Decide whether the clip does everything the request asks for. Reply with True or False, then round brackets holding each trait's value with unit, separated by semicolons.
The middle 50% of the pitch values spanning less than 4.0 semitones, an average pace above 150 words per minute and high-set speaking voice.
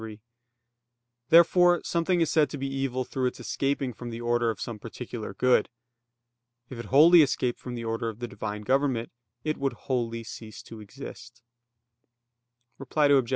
False (3.3 semitones; 165 wpm; 125 Hz)